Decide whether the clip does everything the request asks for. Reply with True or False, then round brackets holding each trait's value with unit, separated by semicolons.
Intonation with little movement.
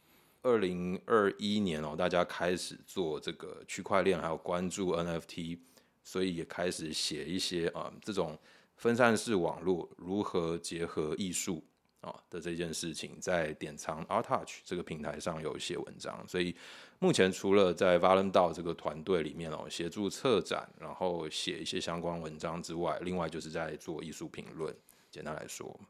True (2.2 semitones)